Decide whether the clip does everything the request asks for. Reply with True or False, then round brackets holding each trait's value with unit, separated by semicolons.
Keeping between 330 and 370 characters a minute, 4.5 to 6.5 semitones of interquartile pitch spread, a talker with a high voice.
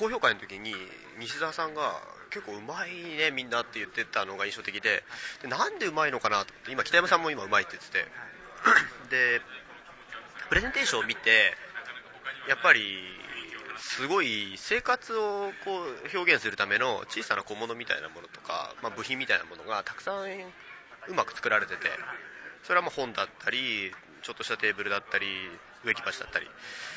False (355 characters per minute; 8.0 semitones; 195 Hz)